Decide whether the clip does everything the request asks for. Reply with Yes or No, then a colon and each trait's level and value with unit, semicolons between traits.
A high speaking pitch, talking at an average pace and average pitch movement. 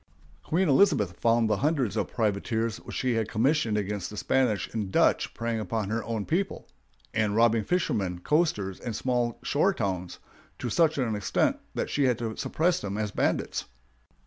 No: low, 115 Hz; average, 170 wpm; average, 3.9 semitones